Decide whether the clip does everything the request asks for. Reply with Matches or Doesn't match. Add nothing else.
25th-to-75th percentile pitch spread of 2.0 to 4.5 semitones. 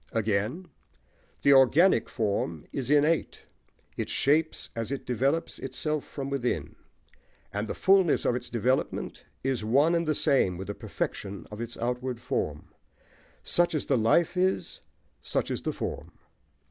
Doesn't match